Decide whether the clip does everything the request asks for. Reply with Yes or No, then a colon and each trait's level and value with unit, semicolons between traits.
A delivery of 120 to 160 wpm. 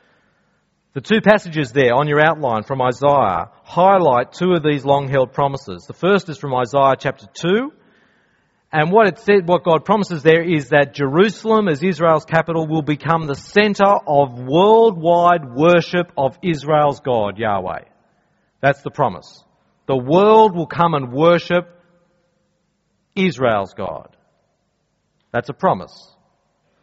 Yes: slow, 135 wpm